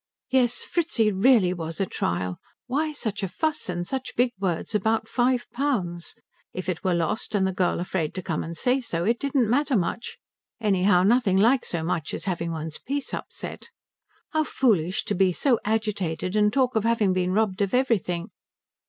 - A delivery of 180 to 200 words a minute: Yes, average, 185 wpm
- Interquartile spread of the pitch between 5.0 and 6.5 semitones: Yes, wide, 5.6 semitones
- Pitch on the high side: Yes, high, 205 Hz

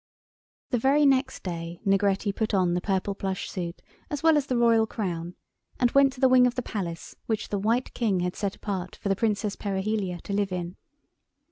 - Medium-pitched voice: No, high, 205 Hz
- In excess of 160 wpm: Yes, fast, 205 wpm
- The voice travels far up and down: No, average, 4.4 semitones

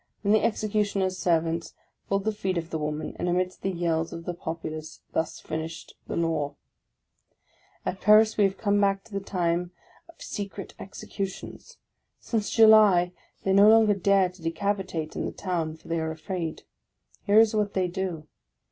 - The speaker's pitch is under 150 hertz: No, medium, 185 Hz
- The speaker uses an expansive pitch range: No, average, 3.4 semitones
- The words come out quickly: No, average, 175 wpm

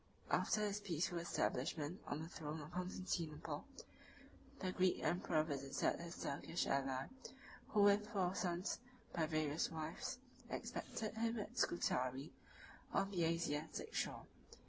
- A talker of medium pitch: Yes, medium, 170 Hz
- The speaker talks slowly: Yes, slow, 125 wpm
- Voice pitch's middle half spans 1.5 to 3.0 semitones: No, average, 4.0 semitones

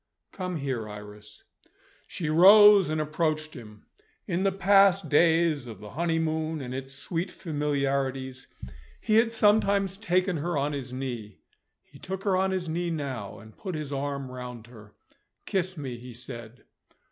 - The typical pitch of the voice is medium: Yes, medium, 155 Hz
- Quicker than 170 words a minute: No, average, 155 wpm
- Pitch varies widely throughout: Yes, wide, 6.3 semitones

